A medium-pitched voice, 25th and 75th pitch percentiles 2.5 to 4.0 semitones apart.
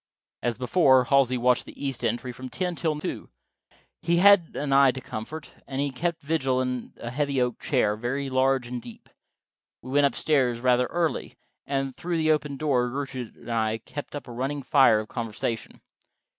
No: low, 130 Hz; average, 2.9 semitones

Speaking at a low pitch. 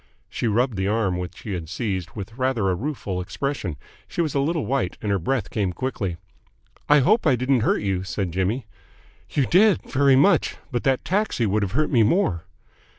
Yes: low, 115 Hz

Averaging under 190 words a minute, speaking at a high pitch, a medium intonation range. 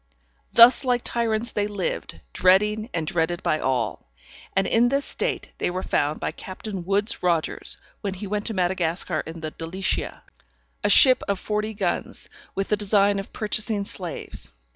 Yes: average, 165 wpm; high, 200 Hz; average, 3.4 semitones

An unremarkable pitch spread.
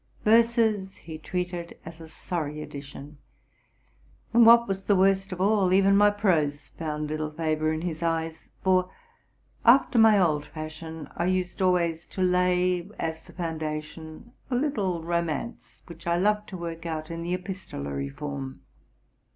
Yes: average, 3.5 semitones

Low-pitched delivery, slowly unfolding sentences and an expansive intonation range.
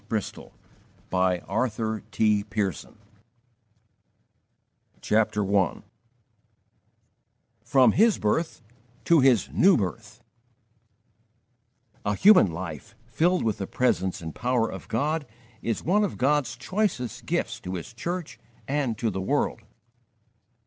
Yes: low, 115 Hz; slow, 105 wpm; wide, 6.9 semitones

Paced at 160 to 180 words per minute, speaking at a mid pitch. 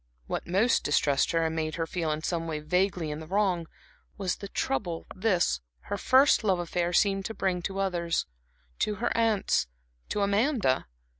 Yes: average, 175 wpm; medium, 180 Hz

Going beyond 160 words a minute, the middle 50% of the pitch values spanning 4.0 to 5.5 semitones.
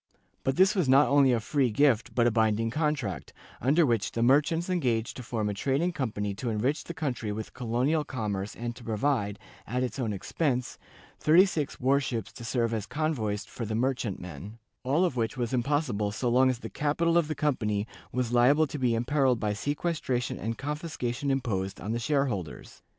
Yes: average, 190 wpm; average, 4.4 semitones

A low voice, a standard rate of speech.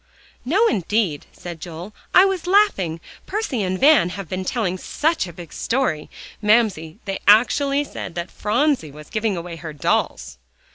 No: high, 195 Hz; average, 155 wpm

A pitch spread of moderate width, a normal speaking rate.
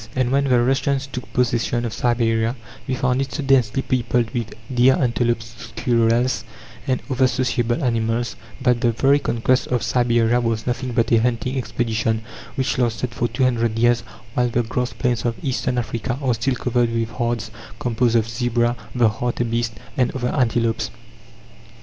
No: narrow, 1.7 semitones; average, 165 wpm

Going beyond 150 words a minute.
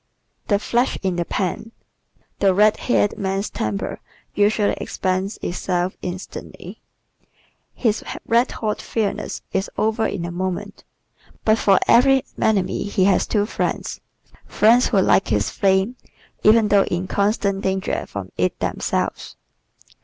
No: slow, 135 wpm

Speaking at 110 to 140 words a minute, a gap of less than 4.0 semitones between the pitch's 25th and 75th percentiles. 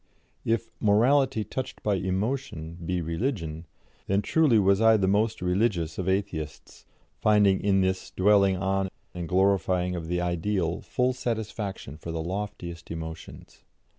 Yes: slow, 135 wpm; average, 3.5 semitones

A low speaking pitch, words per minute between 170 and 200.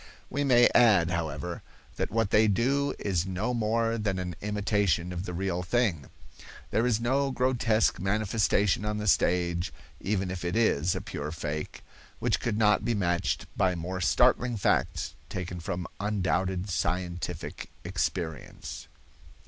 No: very low, 95 Hz; average, 145 wpm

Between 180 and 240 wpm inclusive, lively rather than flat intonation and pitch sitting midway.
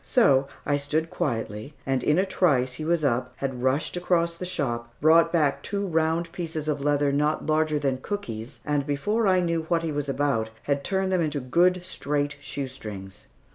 No: average, 185 wpm; average, 3.8 semitones; medium, 150 Hz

